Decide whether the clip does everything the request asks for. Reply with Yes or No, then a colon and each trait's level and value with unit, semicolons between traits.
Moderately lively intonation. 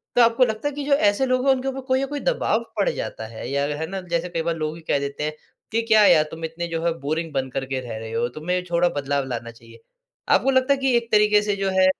No: wide, 8.6 semitones